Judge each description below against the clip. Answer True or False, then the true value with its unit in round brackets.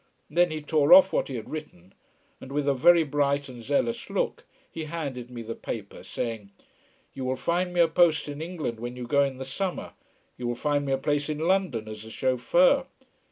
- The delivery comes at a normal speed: False (210 wpm)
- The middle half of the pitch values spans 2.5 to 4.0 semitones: False (5.0 semitones)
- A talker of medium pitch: True (145 Hz)